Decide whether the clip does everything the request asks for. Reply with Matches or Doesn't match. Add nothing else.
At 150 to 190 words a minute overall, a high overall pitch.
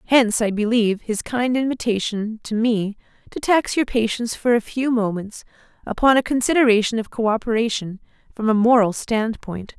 Matches